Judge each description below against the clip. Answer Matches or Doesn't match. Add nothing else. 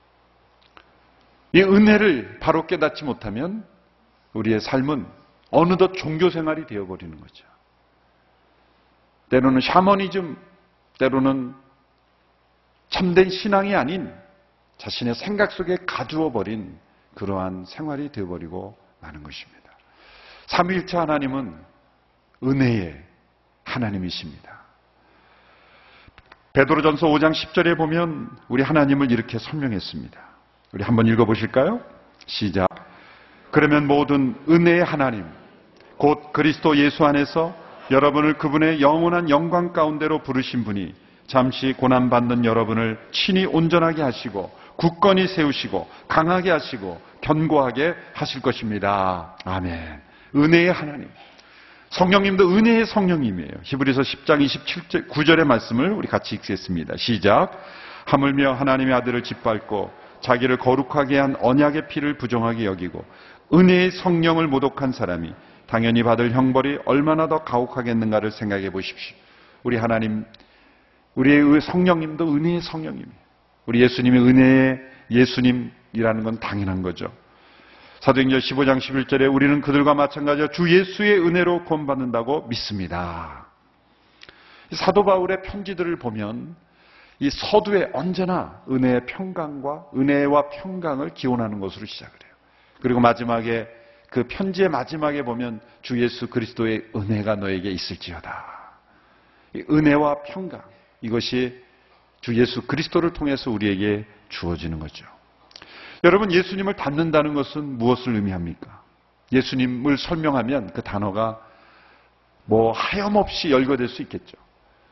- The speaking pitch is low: Matches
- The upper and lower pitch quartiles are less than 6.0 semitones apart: Doesn't match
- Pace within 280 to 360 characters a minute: Matches